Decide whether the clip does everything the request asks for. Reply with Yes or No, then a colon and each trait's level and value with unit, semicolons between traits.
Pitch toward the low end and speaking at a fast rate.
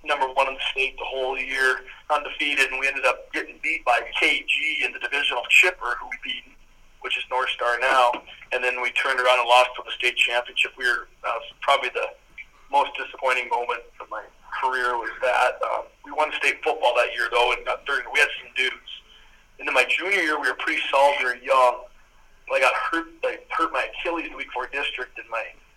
Yes: low, 130 Hz; fast, 215 wpm